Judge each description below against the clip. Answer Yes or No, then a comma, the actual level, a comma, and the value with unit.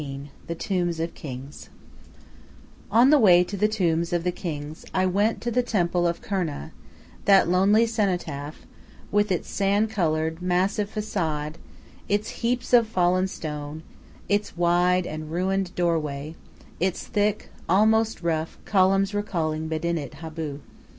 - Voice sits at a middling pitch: Yes, medium, 180 Hz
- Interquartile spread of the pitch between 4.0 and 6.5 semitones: Yes, average, 4.3 semitones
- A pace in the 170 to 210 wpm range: No, average, 140 wpm